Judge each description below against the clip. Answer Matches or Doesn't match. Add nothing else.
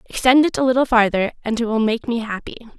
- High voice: Matches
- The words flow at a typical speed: Doesn't match